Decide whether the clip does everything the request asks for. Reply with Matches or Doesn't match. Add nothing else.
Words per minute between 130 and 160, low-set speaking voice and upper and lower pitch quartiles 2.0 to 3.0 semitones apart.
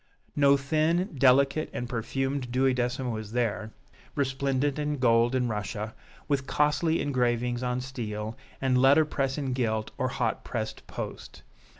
Matches